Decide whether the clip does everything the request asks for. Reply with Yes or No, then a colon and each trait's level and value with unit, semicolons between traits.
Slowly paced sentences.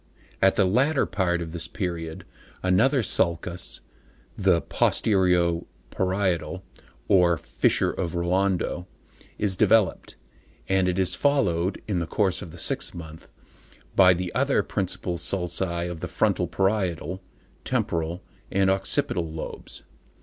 Yes: slow, 125 wpm